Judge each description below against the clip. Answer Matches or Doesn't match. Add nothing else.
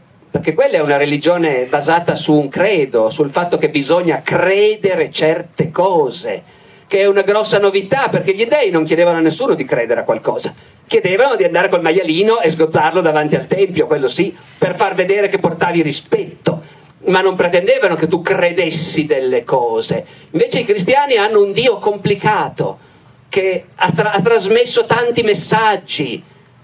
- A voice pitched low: Doesn't match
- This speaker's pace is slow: Doesn't match